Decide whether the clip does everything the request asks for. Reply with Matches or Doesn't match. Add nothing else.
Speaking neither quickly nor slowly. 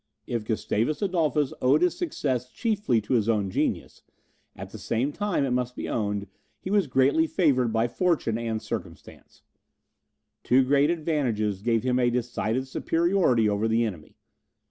Matches